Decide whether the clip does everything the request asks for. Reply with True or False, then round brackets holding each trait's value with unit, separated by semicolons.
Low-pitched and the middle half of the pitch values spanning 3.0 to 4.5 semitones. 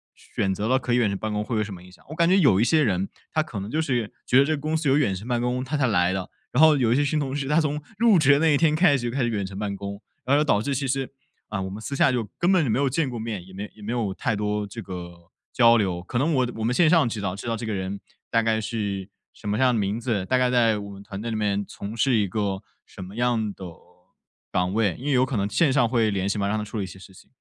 False (115 Hz; 5.0 semitones)